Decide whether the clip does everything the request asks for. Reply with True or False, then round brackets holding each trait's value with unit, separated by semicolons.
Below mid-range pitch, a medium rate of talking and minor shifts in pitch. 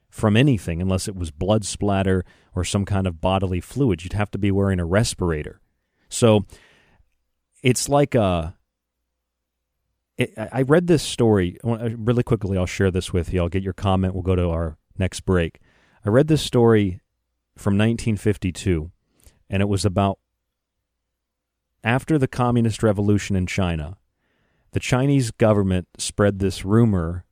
False (95 Hz; 150 wpm; 4.1 semitones)